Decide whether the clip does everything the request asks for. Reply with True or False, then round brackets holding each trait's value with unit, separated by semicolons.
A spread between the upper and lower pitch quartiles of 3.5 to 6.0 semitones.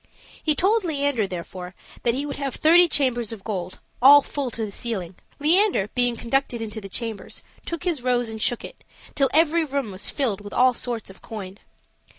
True (5.2 semitones)